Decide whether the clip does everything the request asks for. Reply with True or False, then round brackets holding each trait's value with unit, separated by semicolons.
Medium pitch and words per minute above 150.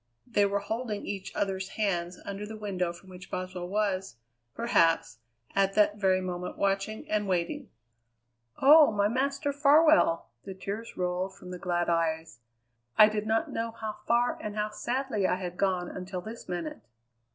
False (195 Hz; 165 wpm)